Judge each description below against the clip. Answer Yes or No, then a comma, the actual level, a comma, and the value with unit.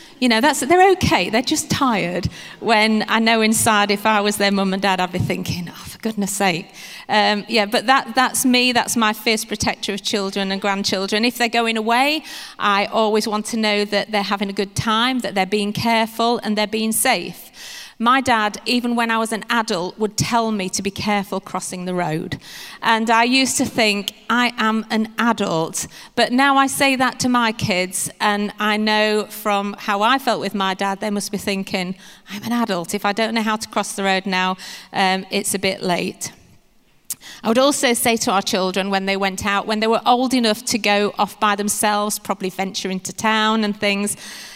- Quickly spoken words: Yes, fast, 210 wpm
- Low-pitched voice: No, high, 210 Hz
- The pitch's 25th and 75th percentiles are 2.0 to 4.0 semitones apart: Yes, narrow, 2.6 semitones